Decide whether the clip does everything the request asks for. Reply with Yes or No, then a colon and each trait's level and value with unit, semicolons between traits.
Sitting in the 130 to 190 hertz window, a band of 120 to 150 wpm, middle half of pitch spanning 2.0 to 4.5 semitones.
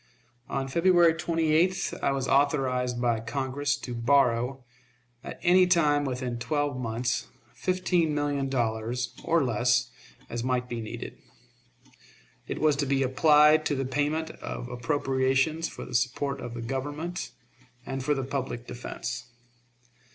Yes: low, 135 Hz; slow, 135 wpm; average, 3.3 semitones